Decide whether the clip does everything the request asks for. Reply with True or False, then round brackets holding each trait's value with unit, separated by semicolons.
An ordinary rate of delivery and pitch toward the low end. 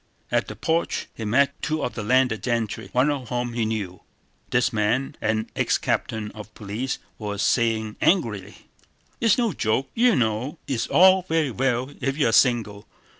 True (170 wpm; 120 Hz)